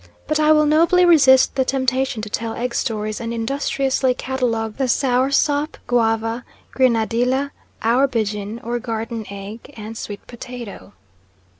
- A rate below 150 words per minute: Yes, average, 140 wpm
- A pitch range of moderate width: Yes, average, 3.1 semitones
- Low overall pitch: No, high, 245 Hz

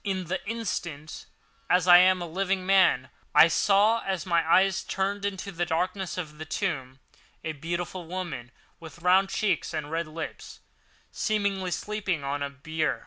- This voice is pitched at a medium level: Yes, medium, 180 Hz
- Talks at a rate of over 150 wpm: Yes, average, 165 wpm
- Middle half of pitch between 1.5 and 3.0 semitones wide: No, average, 3.4 semitones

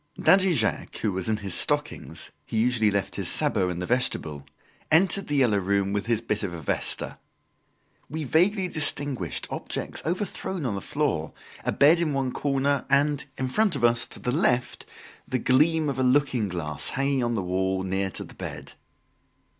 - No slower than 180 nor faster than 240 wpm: Yes, average, 185 wpm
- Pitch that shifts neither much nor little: No, wide, 6.6 semitones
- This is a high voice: No, low, 125 Hz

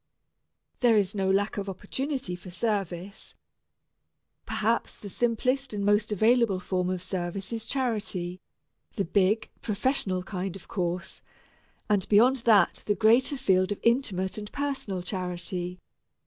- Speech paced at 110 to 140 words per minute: Yes, slow, 135 wpm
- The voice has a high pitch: Yes, high, 200 Hz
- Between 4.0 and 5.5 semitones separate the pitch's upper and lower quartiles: No, average, 3.6 semitones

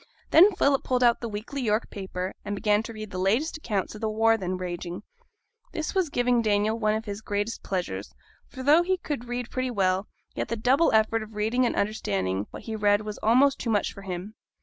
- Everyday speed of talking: No, fast, 215 wpm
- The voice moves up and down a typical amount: Yes, average, 3.4 semitones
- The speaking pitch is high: Yes, high, 220 Hz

